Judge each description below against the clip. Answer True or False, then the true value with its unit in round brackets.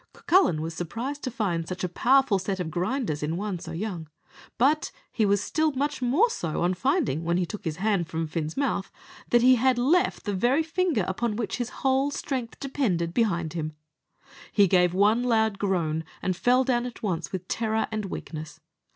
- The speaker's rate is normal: True (195 wpm)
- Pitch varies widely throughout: True (6.8 semitones)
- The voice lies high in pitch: True (210 Hz)